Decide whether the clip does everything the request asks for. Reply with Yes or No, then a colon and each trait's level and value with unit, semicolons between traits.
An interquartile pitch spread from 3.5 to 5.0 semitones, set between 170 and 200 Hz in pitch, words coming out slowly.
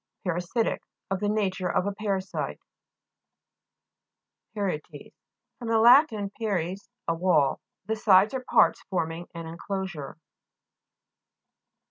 Yes: average, 3.9 semitones; high, 190 Hz; slow, 110 wpm